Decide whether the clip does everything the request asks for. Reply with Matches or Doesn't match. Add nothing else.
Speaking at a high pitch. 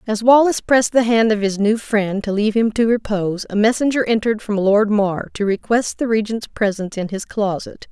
Matches